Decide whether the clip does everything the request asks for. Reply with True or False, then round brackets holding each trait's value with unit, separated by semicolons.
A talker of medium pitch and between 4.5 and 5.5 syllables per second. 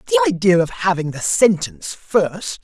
False (200 Hz; 5.2 syllables/s)